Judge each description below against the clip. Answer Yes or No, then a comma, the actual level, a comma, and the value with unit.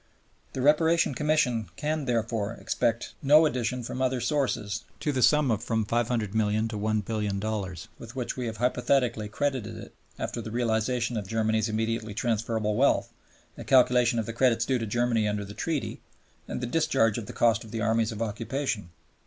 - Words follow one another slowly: No, average, 175 wpm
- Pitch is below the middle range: Yes, low, 115 Hz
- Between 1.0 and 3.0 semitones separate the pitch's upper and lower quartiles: Yes, average, 2.7 semitones